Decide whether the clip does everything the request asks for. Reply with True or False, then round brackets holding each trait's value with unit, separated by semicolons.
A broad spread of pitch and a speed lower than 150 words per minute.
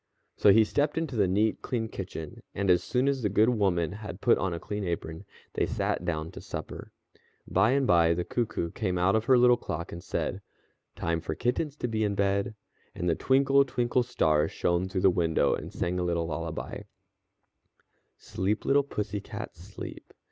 False (5.7 semitones; 190 wpm)